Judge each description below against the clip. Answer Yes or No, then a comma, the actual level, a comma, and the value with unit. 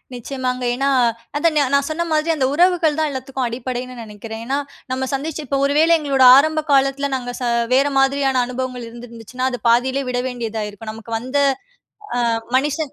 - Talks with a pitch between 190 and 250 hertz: No, very high, 260 Hz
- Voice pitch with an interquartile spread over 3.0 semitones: No, narrow, 2.5 semitones